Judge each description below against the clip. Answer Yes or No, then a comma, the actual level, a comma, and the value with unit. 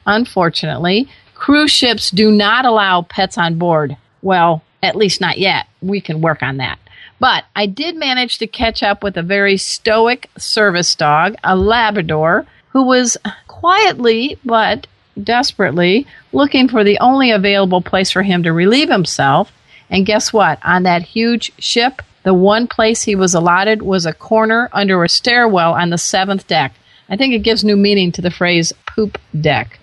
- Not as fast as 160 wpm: No, average, 170 wpm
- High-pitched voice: Yes, high, 200 Hz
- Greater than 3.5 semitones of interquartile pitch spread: Yes, average, 4.5 semitones